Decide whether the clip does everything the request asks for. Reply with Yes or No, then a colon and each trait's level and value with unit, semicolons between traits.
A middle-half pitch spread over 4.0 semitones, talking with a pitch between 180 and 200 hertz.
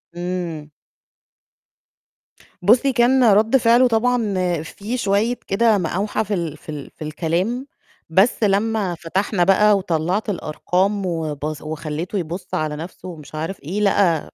Yes: average, 4.9 semitones; high, 190 Hz